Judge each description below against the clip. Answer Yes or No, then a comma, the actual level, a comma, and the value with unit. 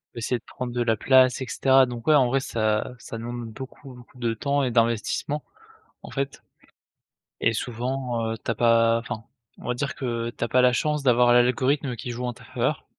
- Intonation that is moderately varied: No, narrow, 2.0 semitones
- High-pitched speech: No, low, 120 Hz